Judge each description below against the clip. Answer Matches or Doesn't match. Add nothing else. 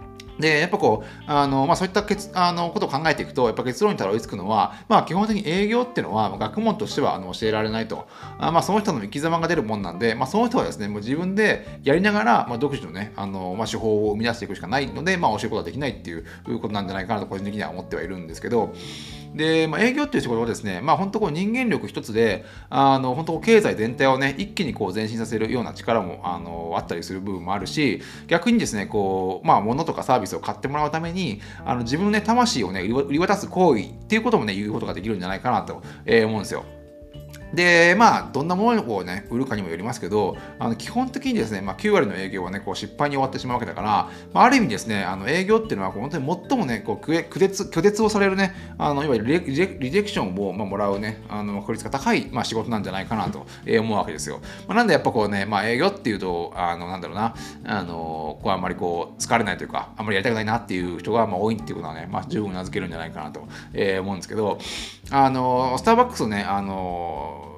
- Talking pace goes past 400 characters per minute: Matches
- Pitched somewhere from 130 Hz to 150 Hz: Doesn't match